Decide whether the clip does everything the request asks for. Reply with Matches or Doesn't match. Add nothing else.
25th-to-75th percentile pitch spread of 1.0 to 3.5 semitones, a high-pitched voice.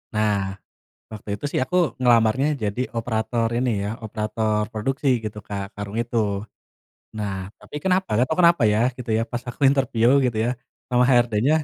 Doesn't match